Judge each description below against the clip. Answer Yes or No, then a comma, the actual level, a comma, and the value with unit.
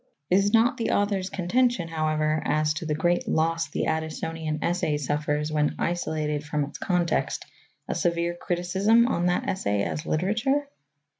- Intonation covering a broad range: No, average, 3.5 semitones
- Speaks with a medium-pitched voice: Yes, medium, 170 Hz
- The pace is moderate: Yes, average, 150 wpm